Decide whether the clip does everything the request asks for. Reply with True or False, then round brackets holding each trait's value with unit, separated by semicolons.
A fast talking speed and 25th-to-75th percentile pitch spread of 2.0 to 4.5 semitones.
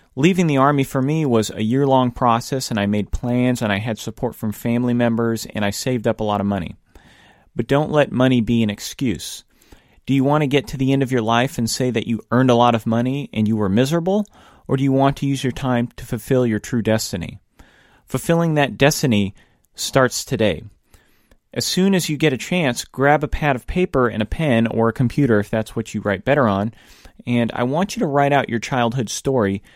True (230 wpm; 3.7 semitones)